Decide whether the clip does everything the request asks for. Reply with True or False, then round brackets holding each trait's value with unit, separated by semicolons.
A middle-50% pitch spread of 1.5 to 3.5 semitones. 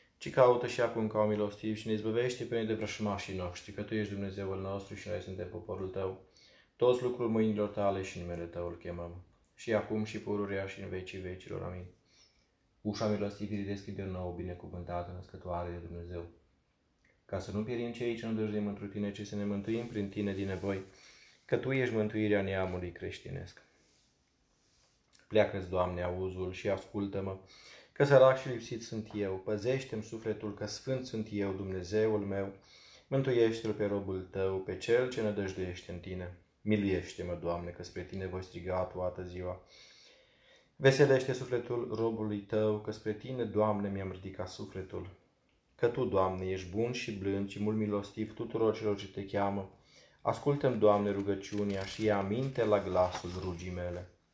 True (2.8 semitones)